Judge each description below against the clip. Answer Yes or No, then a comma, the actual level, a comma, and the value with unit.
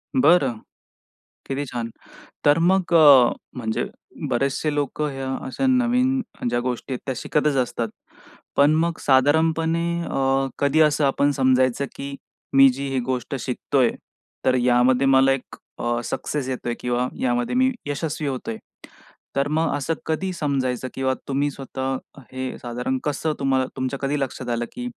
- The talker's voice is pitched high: No, low, 135 Hz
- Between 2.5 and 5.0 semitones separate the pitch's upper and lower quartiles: Yes, average, 2.9 semitones